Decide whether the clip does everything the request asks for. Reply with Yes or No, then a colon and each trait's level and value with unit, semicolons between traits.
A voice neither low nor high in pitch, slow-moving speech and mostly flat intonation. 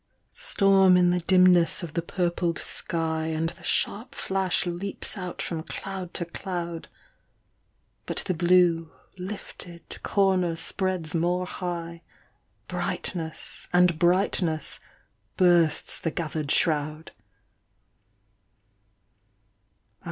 Yes: medium, 175 Hz; slow, 100 wpm; narrow, 1.8 semitones